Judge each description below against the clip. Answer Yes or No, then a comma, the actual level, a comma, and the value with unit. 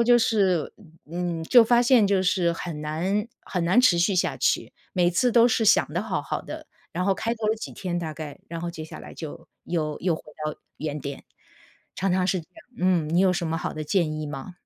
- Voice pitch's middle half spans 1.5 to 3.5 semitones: No, average, 3.9 semitones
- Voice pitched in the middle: Yes, medium, 175 Hz